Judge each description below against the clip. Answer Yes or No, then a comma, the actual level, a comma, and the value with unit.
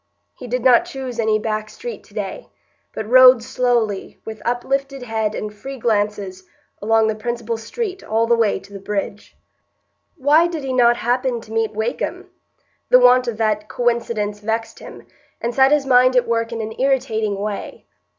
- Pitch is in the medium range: No, high, 230 Hz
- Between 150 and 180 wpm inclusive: Yes, average, 175 wpm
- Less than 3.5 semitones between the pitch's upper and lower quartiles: Yes, average, 2.9 semitones